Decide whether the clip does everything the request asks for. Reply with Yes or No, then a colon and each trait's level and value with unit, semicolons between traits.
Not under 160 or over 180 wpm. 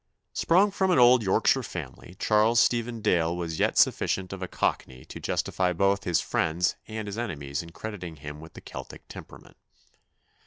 Yes: average, 170 wpm